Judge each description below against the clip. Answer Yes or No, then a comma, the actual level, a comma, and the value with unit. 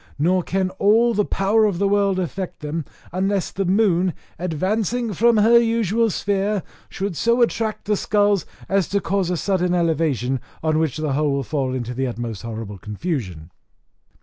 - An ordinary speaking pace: Yes, average, 175 wpm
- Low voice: No, medium, 185 Hz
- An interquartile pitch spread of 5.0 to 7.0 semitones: Yes, average, 5.3 semitones